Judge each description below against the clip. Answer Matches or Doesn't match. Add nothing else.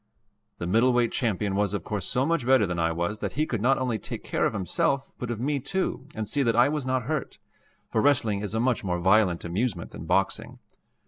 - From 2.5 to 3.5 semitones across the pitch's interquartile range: Doesn't match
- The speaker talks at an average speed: Doesn't match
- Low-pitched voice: Matches